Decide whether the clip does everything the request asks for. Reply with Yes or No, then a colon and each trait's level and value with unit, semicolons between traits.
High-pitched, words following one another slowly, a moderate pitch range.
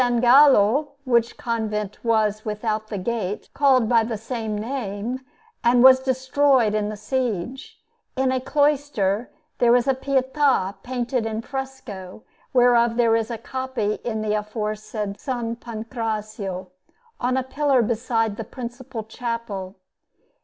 Yes: high, 235 Hz; slow, 130 wpm; average, 3.3 semitones